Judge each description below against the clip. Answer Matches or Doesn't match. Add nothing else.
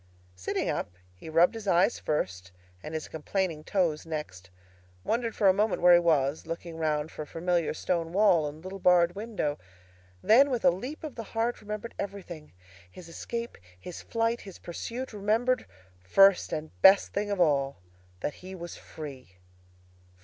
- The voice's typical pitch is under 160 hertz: Doesn't match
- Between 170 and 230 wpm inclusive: Doesn't match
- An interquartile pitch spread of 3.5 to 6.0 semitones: Matches